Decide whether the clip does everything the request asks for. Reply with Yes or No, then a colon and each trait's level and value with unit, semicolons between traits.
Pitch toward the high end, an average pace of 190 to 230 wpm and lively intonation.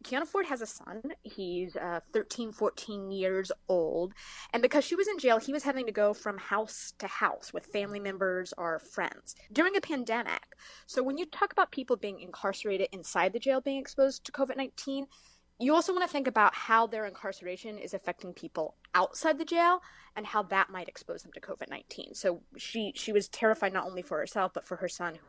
Yes: high, 220 Hz; average, 200 wpm; wide, 6.4 semitones